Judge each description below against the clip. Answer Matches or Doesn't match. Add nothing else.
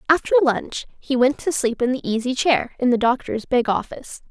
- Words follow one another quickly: Matches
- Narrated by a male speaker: Doesn't match